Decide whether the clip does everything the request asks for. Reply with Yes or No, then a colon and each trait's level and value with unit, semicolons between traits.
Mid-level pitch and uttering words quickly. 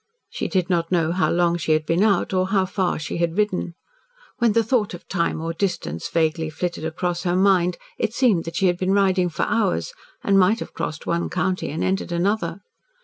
Yes: medium, 180 Hz; fast, 210 wpm